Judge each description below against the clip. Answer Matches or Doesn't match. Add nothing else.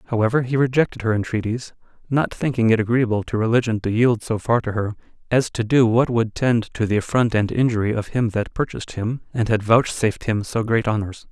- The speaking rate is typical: Doesn't match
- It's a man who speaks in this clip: Matches